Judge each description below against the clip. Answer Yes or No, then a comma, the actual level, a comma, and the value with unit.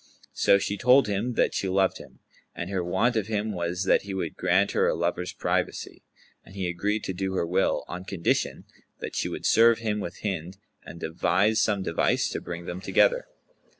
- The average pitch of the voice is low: Yes, very low, 95 Hz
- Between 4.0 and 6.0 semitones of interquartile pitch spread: No, average, 2.9 semitones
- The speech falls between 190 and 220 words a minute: Yes, average, 200 wpm